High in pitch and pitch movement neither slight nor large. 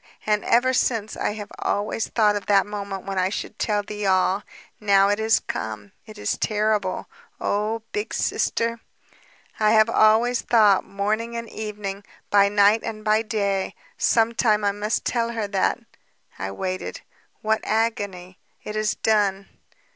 No: high, 210 Hz; narrow, 1.7 semitones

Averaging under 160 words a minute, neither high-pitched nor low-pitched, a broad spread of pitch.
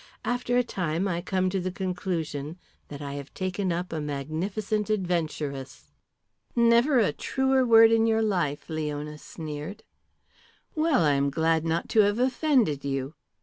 Yes: average, 150 wpm; medium, 180 Hz; wide, 6.6 semitones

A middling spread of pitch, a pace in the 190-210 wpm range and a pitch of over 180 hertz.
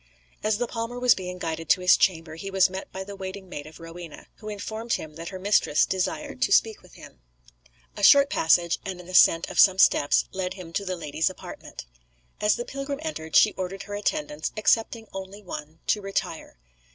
Yes: average, 4.1 semitones; average, 200 wpm; high, 190 Hz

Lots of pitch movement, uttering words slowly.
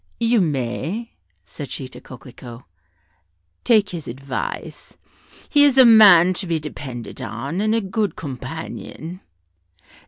Yes: wide, 8.4 semitones; slow, 125 wpm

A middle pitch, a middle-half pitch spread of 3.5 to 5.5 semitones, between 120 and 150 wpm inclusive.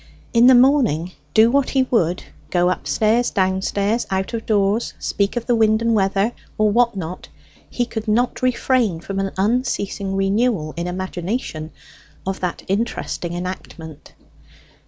No: high, 205 Hz; average, 4.0 semitones; average, 145 wpm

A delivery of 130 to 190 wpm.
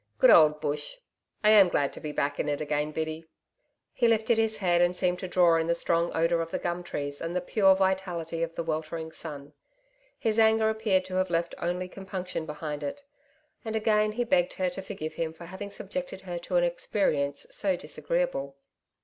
No: average, 200 wpm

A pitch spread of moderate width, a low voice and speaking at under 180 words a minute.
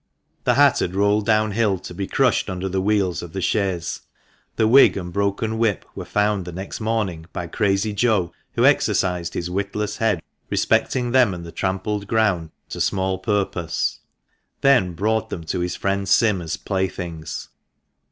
Yes: average, 3.1 semitones; very low, 95 Hz; average, 165 wpm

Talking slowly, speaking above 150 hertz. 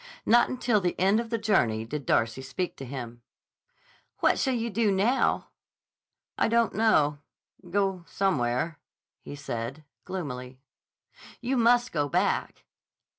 Yes: slow, 130 wpm; medium, 185 Hz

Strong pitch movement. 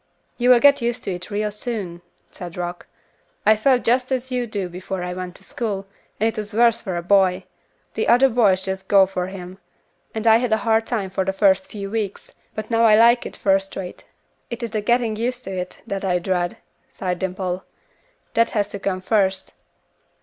No: average, 3.6 semitones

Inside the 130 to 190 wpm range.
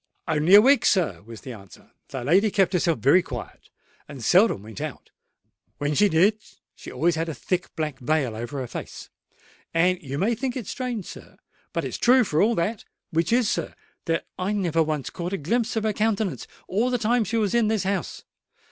No: average, 200 wpm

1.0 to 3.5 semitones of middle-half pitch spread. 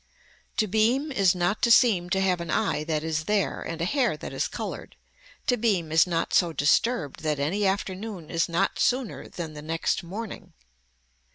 No: average, 4.8 semitones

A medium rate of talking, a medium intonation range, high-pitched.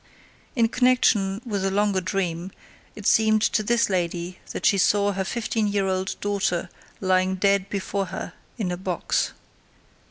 No: average, 155 wpm; narrow, 2.0 semitones; high, 195 Hz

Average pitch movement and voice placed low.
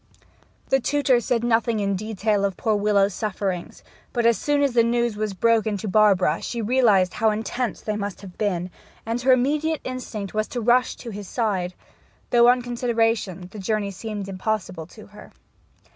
No: average, 3.1 semitones; high, 215 Hz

